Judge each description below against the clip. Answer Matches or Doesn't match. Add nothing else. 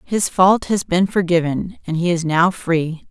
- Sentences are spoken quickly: Doesn't match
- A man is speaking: Doesn't match